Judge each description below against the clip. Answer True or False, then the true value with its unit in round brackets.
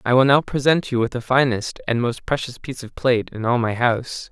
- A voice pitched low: True (125 Hz)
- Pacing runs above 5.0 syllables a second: True (5.7 syllables/s)